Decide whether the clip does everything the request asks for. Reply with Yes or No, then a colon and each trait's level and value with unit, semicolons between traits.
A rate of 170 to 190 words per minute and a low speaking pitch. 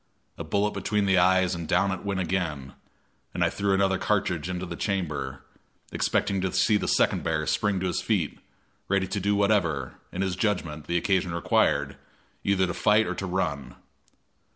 Yes: average, 180 wpm; very low, 95 Hz